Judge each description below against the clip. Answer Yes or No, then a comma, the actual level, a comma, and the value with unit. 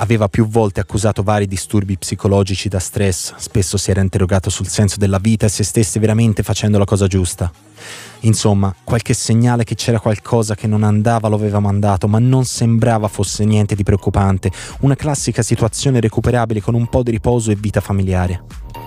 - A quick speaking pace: Yes, fast, 180 wpm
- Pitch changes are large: No, narrow, 2.4 semitones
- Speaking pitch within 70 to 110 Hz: Yes, low, 105 Hz